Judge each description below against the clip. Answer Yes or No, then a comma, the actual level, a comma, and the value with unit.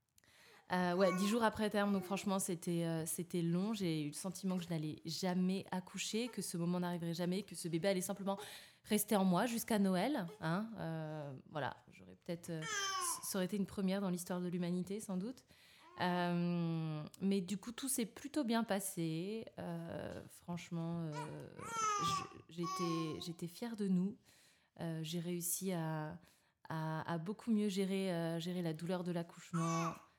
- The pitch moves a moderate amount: Yes, average, 3.1 semitones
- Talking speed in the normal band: Yes, average, 165 wpm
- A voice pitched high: No, medium, 180 Hz